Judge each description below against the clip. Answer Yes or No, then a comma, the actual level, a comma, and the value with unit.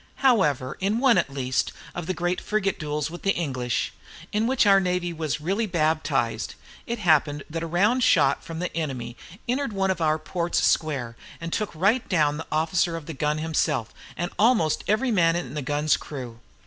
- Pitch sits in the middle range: Yes, medium, 165 Hz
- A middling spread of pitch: Yes, average, 4.6 semitones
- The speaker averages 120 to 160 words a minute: No, average, 200 wpm